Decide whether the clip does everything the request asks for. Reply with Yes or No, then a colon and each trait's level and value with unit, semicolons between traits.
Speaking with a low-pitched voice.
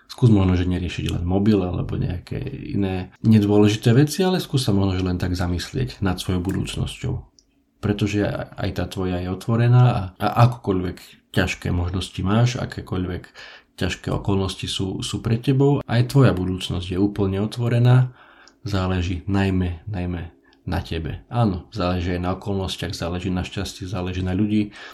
Yes: low, 100 Hz